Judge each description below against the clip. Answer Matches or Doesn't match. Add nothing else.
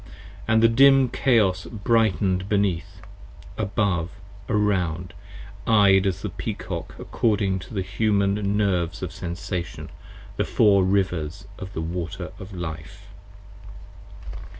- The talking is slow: Matches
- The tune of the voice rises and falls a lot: Doesn't match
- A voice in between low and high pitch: Doesn't match